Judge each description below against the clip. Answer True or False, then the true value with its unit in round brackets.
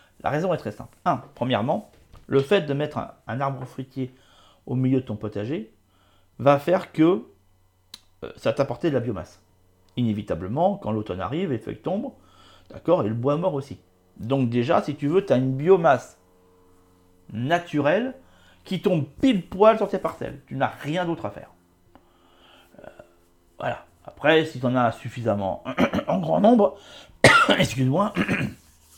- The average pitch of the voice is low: True (120 Hz)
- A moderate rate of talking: True (160 wpm)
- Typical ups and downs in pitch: False (7.8 semitones)